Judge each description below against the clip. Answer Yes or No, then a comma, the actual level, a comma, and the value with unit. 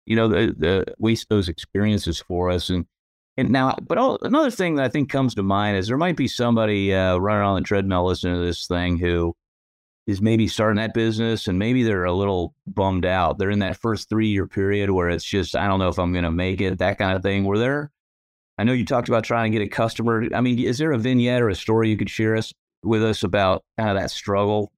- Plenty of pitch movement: No, average, 3.7 semitones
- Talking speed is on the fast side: Yes, fast, 245 wpm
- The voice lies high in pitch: No, low, 105 Hz